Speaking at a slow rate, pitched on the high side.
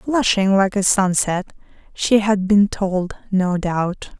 Yes: slow, 130 wpm; high, 195 Hz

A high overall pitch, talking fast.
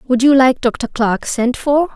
Yes: very high, 255 Hz; fast, 215 wpm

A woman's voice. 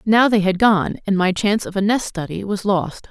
Yes: female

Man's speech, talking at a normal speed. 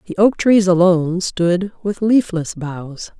No: female; average, 150 wpm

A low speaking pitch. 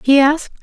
No: very high, 285 Hz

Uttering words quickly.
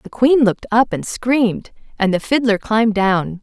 No: average, 195 wpm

